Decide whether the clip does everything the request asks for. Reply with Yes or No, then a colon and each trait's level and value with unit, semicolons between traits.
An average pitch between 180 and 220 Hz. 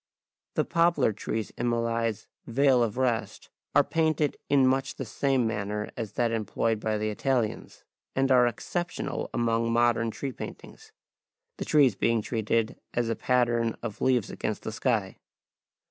No: low, 115 Hz